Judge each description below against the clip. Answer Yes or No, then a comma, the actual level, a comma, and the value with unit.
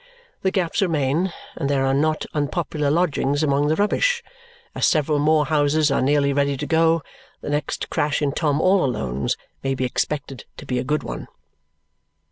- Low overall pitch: No, medium, 145 Hz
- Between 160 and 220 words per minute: Yes, average, 175 wpm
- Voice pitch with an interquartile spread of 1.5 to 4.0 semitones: Yes, narrow, 2.5 semitones